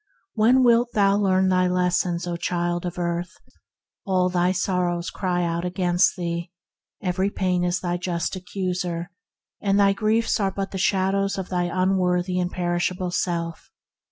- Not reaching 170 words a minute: Yes, average, 155 wpm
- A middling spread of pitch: No, narrow, 1.6 semitones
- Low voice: No, medium, 180 Hz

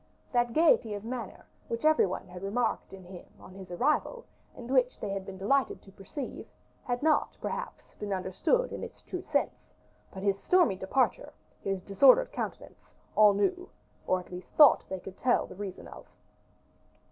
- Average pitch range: No, wide, 5.8 semitones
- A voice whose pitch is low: No, high, 205 Hz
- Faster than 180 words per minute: No, average, 175 wpm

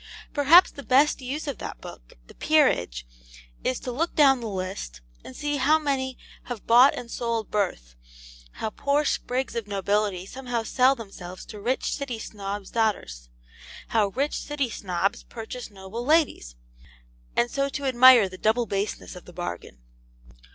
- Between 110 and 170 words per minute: Yes, average, 160 wpm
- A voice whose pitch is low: No, high, 230 Hz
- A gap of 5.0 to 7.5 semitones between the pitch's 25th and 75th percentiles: Yes, wide, 5.4 semitones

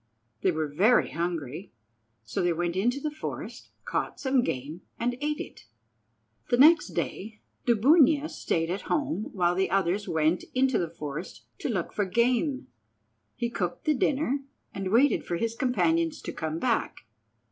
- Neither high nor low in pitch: No, high, 200 Hz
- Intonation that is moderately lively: No, wide, 7.2 semitones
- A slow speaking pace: No, average, 160 wpm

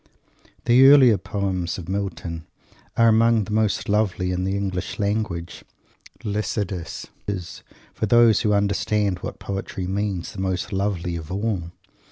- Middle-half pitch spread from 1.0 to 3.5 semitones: Yes, average, 2.7 semitones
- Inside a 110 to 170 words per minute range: Yes, average, 140 wpm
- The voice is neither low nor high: No, low, 100 Hz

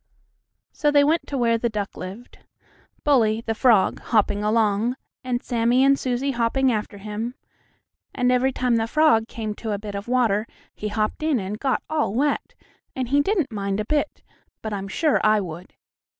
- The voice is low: No, high, 230 Hz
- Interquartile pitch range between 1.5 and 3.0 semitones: No, average, 3.9 semitones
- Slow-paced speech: No, average, 185 wpm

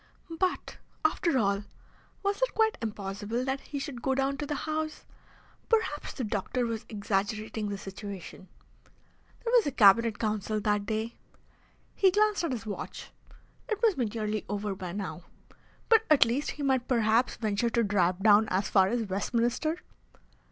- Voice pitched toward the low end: No, high, 230 Hz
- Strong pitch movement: Yes, wide, 5.7 semitones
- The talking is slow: No, average, 160 wpm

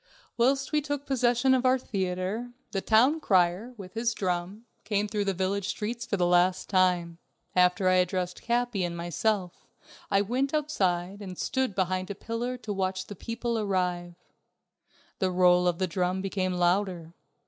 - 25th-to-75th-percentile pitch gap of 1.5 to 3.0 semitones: No, average, 4.4 semitones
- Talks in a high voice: Yes, high, 195 Hz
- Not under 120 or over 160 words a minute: No, average, 170 wpm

